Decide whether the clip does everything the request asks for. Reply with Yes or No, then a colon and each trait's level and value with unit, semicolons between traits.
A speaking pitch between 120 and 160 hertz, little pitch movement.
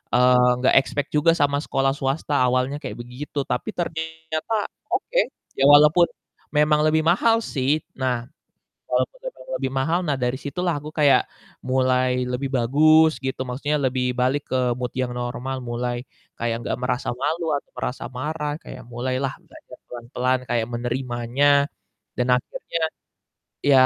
No: low, 135 Hz; average, 3.2 semitones